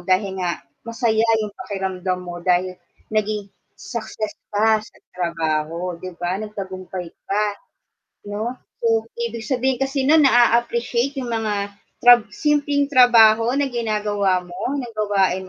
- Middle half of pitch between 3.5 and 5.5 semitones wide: Yes, average, 4.1 semitones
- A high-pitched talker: Yes, high, 215 Hz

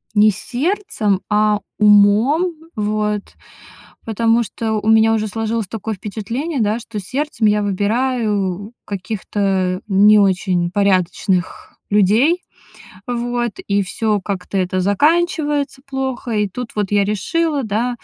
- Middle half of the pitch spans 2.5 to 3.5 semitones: Yes, average, 3.2 semitones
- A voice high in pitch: Yes, high, 215 Hz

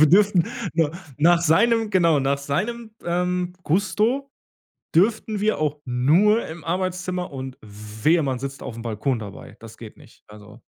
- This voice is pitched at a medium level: Yes, medium, 170 Hz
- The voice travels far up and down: Yes, wide, 6.2 semitones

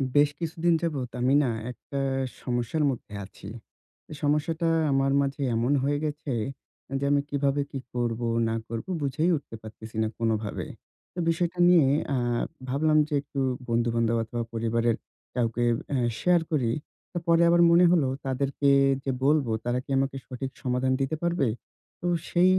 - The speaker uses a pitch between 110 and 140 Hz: Yes, low, 135 Hz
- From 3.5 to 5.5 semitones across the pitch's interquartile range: Yes, average, 4.5 semitones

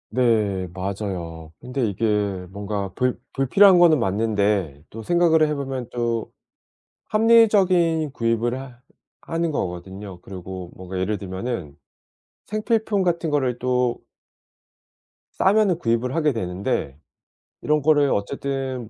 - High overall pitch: No, low, 120 Hz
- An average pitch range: No, wide, 7.7 semitones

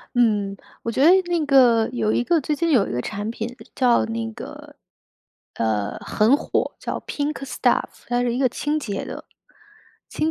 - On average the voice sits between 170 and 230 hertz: No, high, 240 Hz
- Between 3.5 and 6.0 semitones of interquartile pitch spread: Yes, average, 5.3 semitones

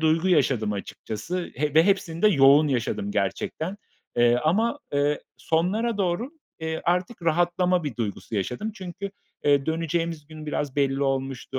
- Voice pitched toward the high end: No, medium, 160 Hz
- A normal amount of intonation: Yes, average, 4.7 semitones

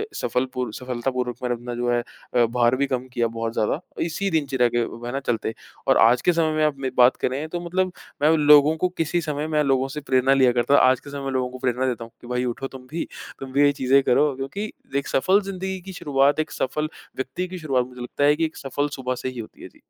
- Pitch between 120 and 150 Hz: Yes, low, 135 Hz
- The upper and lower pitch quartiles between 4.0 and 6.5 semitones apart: No, average, 3.3 semitones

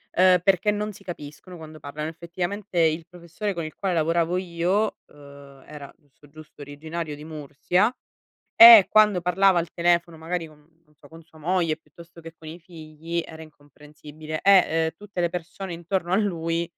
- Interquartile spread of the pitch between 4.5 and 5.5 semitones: No, narrow, 2.6 semitones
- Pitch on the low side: No, medium, 170 Hz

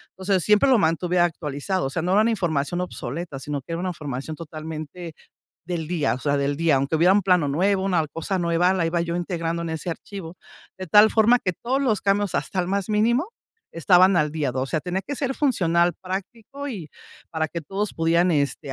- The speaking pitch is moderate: Yes, medium, 175 Hz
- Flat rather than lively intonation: No, average, 3.6 semitones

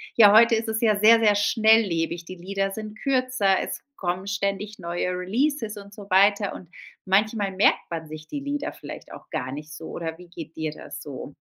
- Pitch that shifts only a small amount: No, average, 4.1 semitones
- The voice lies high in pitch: Yes, high, 200 Hz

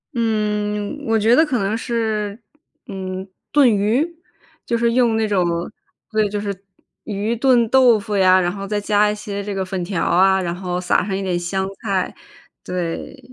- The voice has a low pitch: No, high, 205 Hz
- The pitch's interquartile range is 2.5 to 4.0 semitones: Yes, average, 2.8 semitones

